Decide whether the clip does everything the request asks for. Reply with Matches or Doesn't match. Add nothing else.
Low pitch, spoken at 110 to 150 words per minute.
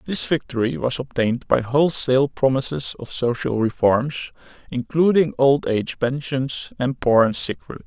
Matches